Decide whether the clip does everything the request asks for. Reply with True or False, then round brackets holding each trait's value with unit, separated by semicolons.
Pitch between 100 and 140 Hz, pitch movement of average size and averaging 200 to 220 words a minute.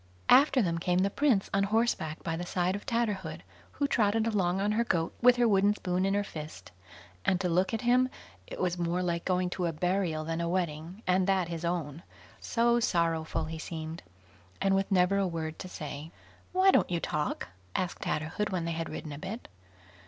False (180 Hz; 3.5 semitones; 205 wpm)